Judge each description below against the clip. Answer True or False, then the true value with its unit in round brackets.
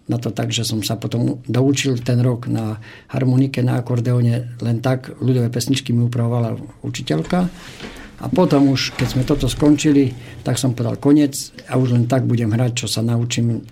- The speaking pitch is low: True (125 Hz)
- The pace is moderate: False (180 wpm)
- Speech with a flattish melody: True (2.3 semitones)